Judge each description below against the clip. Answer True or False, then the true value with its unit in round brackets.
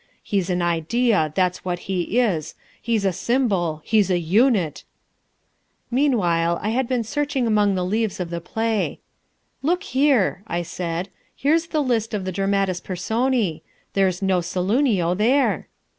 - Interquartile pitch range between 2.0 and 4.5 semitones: False (5.1 semitones)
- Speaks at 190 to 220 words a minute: False (150 wpm)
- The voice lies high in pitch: True (195 Hz)